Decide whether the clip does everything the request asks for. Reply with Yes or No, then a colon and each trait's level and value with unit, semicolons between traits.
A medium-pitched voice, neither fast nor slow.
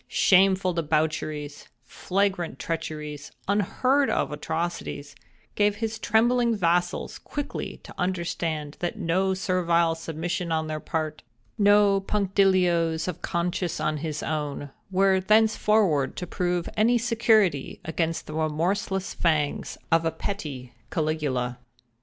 No: medium, 170 Hz; slow, 100 wpm